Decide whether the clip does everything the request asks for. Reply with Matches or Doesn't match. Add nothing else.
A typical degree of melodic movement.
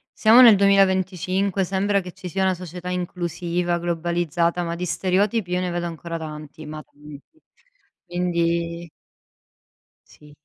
Doesn't match